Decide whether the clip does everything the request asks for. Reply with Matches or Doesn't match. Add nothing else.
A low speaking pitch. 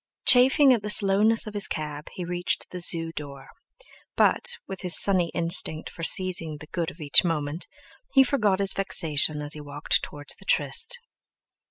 Doesn't match